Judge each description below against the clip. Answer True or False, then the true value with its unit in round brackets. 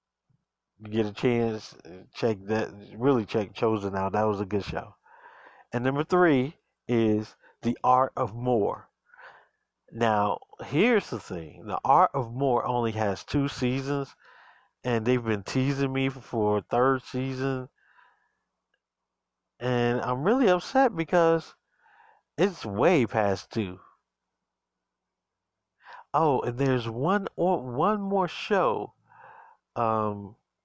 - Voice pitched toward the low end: True (125 Hz)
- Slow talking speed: True (115 wpm)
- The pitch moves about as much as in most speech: True (4.5 semitones)